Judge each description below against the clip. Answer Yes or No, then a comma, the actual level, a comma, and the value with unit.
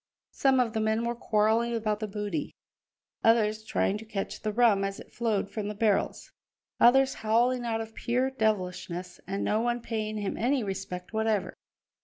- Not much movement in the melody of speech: Yes, narrow, 2.2 semitones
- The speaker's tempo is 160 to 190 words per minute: Yes, average, 175 wpm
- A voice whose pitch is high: Yes, high, 220 Hz